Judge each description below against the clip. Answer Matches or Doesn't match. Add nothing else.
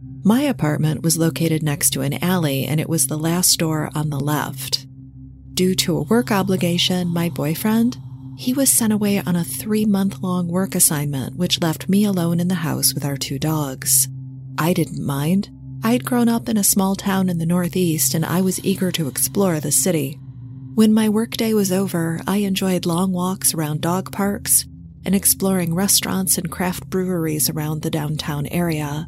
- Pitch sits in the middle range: Matches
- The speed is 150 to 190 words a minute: Matches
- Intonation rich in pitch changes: Doesn't match